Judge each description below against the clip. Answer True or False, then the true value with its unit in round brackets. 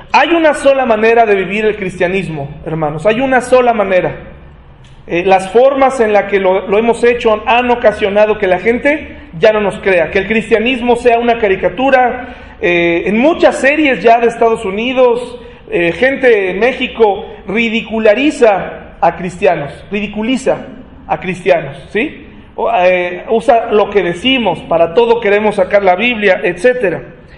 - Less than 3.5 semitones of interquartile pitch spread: False (4.6 semitones)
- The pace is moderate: True (155 wpm)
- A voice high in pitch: True (215 Hz)